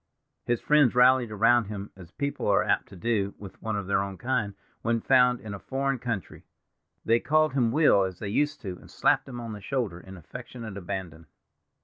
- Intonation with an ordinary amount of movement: Yes, average, 4.2 semitones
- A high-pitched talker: No, low, 110 Hz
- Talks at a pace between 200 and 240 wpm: Yes, fast, 205 wpm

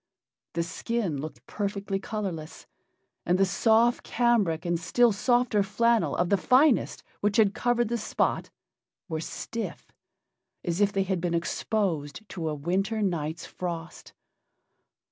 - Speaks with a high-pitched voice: Yes, high, 195 Hz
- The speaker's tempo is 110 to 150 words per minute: Yes, slow, 135 wpm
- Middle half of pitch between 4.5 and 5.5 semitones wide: Yes, average, 4.8 semitones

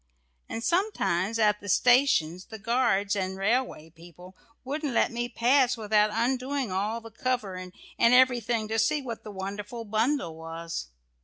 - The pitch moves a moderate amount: Yes, average, 4.5 semitones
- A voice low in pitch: No, high, 225 Hz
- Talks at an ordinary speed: Yes, average, 150 wpm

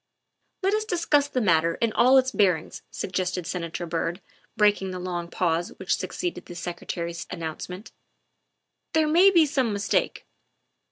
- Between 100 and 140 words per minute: No, average, 160 wpm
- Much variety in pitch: Yes, wide, 7.7 semitones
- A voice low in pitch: No, medium, 185 Hz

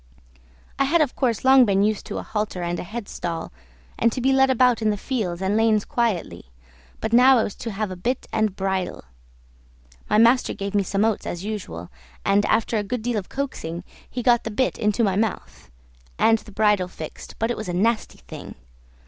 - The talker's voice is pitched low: No, high, 215 Hz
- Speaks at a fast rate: Yes, fast, 210 wpm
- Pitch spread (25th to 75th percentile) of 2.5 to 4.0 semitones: Yes, average, 3.4 semitones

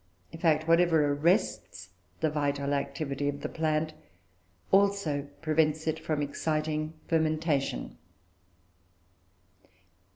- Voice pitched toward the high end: No, medium, 155 Hz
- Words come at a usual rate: No, slow, 95 wpm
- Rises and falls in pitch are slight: Yes, narrow, 2.0 semitones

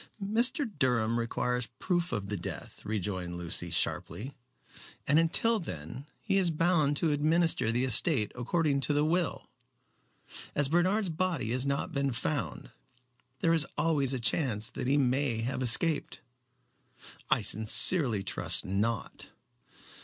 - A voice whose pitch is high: No, medium, 140 Hz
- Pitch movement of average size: No, wide, 6.4 semitones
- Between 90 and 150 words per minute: Yes, slow, 135 wpm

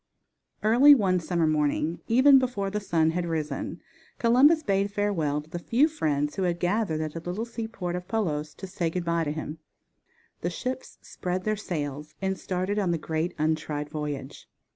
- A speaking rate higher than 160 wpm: Yes, average, 180 wpm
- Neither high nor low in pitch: Yes, medium, 180 Hz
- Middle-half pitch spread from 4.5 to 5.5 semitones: Yes, average, 5.0 semitones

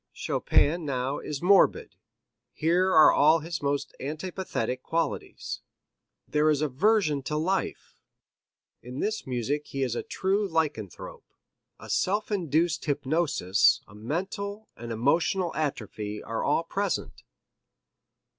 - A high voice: No, medium, 155 Hz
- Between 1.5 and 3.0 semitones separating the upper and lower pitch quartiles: No, average, 5.1 semitones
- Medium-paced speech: No, slow, 115 wpm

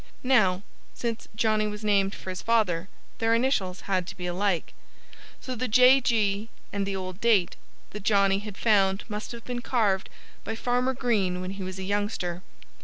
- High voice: Yes, high, 205 Hz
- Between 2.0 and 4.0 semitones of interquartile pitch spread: Yes, average, 3.3 semitones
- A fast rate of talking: No, average, 180 wpm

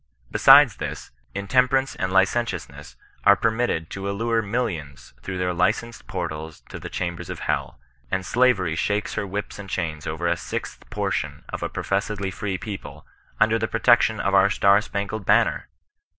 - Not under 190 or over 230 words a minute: No, average, 165 wpm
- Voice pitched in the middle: No, low, 100 Hz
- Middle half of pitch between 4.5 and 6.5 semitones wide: No, average, 3.7 semitones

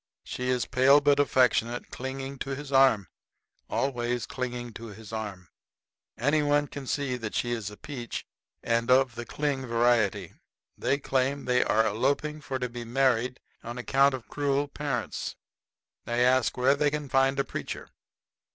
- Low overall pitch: Yes, low, 130 Hz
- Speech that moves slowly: No, average, 160 wpm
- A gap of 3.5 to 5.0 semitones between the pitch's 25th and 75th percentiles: No, average, 2.7 semitones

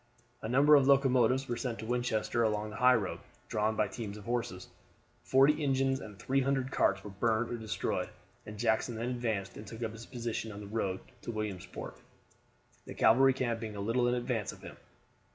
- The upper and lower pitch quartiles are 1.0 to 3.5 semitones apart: Yes, average, 3.0 semitones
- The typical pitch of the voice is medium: No, low, 115 Hz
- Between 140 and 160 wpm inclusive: No, average, 190 wpm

